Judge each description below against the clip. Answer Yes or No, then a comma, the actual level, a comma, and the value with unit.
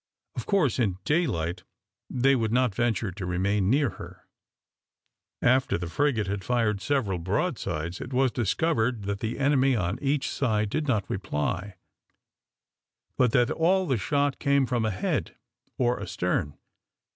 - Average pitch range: No, wide, 5.7 semitones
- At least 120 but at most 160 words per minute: Yes, average, 145 wpm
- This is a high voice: No, low, 115 Hz